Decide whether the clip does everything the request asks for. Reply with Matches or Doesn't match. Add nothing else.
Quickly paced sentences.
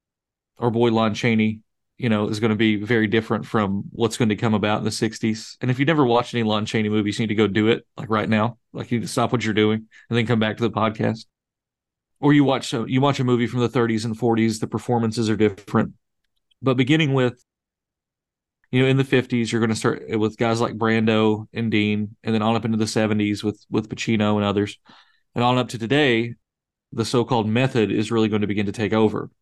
Matches